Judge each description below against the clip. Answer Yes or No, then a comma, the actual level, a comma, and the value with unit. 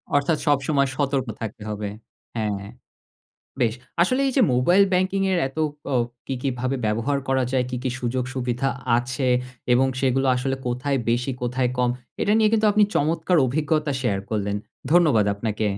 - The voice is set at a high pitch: No, low, 130 Hz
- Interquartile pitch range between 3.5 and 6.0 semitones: Yes, average, 3.8 semitones